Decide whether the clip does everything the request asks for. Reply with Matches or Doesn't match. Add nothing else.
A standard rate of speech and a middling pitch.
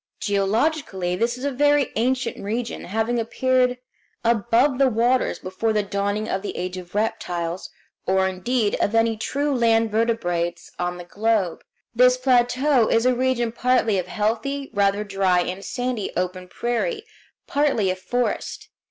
Doesn't match